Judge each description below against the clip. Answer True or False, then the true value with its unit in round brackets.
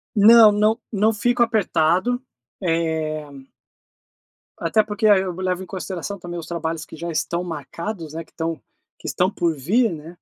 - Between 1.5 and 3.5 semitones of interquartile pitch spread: False (4.3 semitones)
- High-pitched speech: False (180 Hz)